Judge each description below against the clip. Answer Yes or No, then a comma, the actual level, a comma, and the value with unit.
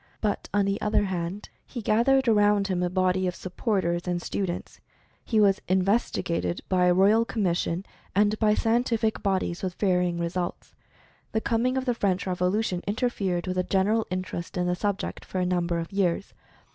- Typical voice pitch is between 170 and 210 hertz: Yes, high, 190 Hz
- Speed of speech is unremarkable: Yes, average, 180 wpm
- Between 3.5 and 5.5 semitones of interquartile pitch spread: No, average, 3.0 semitones